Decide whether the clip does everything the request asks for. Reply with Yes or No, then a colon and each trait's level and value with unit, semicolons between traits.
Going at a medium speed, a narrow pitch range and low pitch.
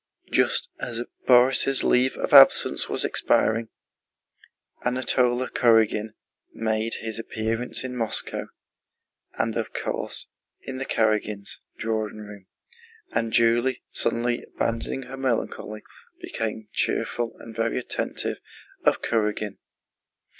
No: slow, 105 wpm; narrow, 2.1 semitones; low, 115 Hz